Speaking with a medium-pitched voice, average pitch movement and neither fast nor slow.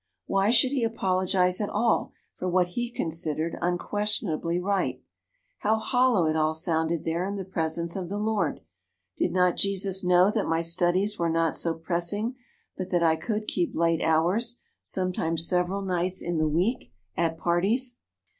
Yes: medium, 180 Hz; average, 3.5 semitones; average, 165 wpm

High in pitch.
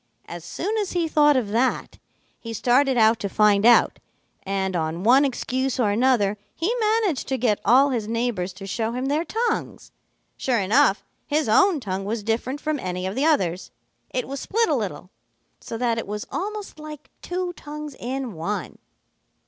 Yes: high, 245 Hz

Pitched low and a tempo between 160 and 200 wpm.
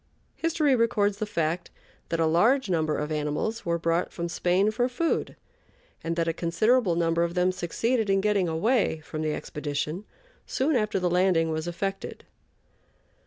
No: medium, 180 Hz; average, 165 wpm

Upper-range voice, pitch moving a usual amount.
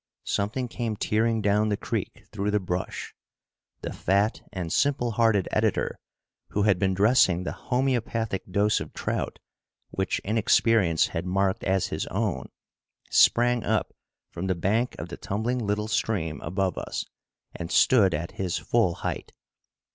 No: low, 105 Hz; average, 3.4 semitones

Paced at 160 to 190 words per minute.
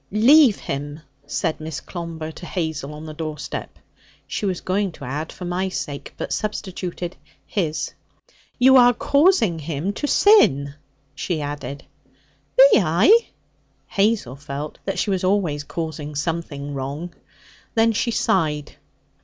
No: slow, 135 wpm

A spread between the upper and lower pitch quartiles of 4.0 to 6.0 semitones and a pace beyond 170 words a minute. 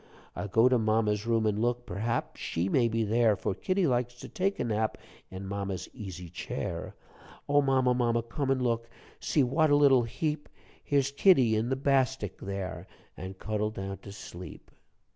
Yes: average, 4.4 semitones; average, 180 wpm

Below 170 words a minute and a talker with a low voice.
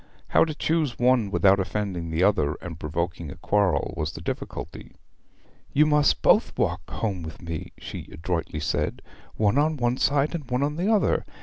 No: average, 180 wpm; low, 100 Hz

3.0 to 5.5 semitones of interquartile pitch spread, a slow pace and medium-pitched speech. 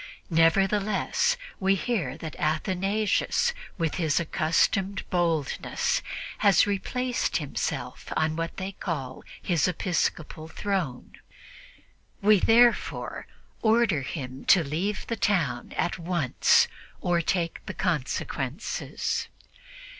Yes: average, 4.3 semitones; slow, 100 wpm; medium, 175 Hz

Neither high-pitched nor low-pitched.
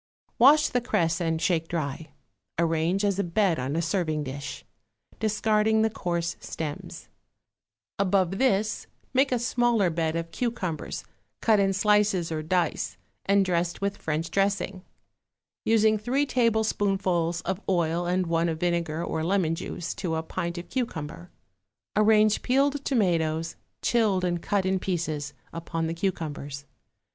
Yes: medium, 180 Hz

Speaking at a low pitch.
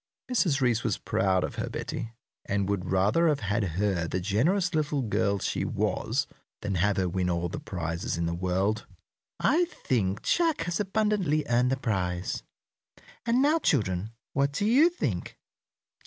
Yes: low, 110 Hz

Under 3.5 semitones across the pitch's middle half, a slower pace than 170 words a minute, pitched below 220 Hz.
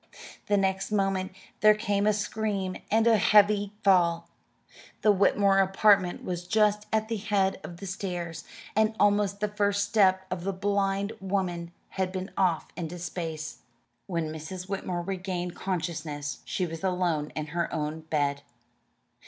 Yes: average, 2.8 semitones; average, 150 wpm; high, 190 Hz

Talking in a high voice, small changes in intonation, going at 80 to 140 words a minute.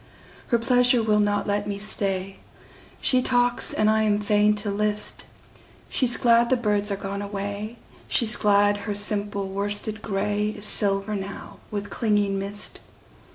Yes: high, 205 Hz; narrow, 1.2 semitones; slow, 135 wpm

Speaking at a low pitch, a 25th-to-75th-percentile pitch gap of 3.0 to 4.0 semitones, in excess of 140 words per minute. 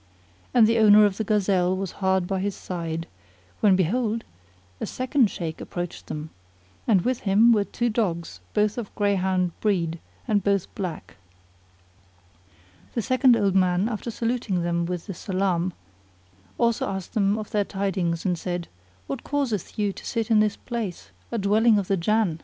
No: high, 200 Hz; average, 3.4 semitones; average, 165 wpm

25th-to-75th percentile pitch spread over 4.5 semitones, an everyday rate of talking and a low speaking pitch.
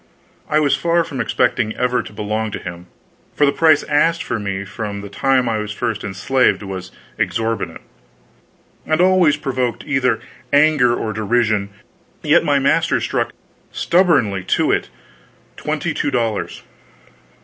Yes: wide, 5.5 semitones; average, 145 wpm; low, 120 Hz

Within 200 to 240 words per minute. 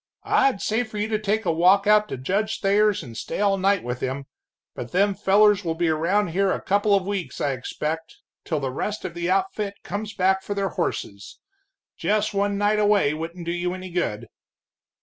Yes: fast, 205 wpm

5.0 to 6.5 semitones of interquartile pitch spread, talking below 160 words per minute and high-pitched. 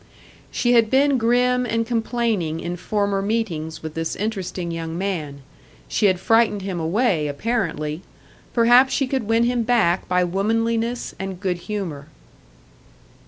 Yes: average, 5.3 semitones; average, 140 wpm; high, 205 Hz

